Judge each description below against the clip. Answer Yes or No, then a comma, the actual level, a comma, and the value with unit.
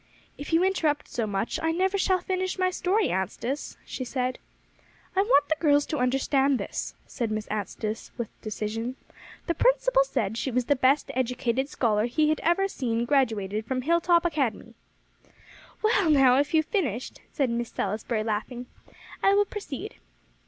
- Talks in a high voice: Yes, very high, 270 Hz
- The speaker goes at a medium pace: Yes, average, 165 wpm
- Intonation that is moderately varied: No, wide, 6.5 semitones